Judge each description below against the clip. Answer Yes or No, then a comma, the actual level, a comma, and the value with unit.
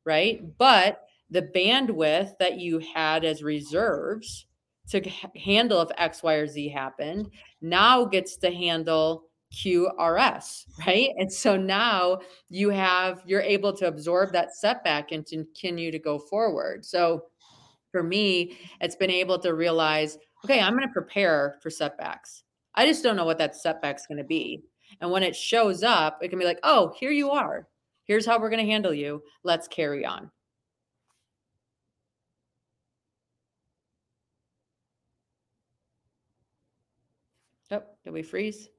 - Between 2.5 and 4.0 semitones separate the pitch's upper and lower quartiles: No, average, 4.5 semitones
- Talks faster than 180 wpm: No, average, 145 wpm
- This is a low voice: No, medium, 175 Hz